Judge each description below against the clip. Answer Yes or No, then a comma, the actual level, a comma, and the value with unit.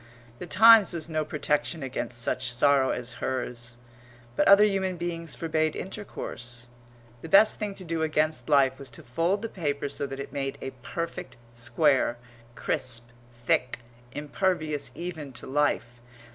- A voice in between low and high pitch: Yes, medium, 145 Hz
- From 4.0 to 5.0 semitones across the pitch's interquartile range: Yes, average, 4.6 semitones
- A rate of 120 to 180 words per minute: Yes, average, 150 wpm